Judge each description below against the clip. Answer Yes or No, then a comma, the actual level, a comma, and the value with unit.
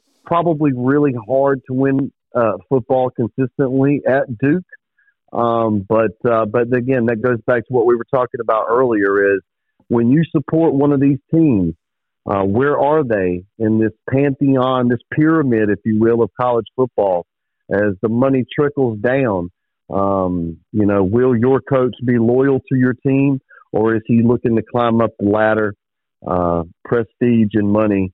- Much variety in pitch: No, average, 3.8 semitones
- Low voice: Yes, low, 120 Hz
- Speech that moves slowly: No, average, 165 wpm